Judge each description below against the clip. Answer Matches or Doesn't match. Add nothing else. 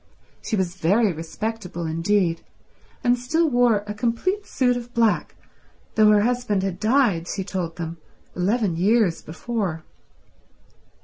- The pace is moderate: Doesn't match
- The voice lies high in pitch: Matches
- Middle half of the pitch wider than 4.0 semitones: Matches